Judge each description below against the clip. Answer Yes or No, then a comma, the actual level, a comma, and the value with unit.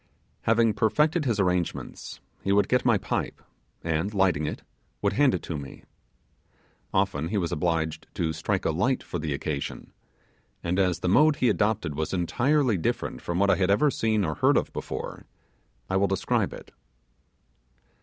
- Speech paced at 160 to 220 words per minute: Yes, average, 170 wpm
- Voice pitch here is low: Yes, very low, 95 Hz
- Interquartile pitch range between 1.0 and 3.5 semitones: No, average, 5.1 semitones